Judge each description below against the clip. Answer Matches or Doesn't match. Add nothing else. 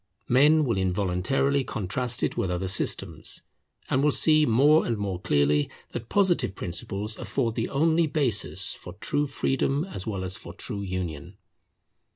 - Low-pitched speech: Matches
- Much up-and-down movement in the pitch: Matches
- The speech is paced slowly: Doesn't match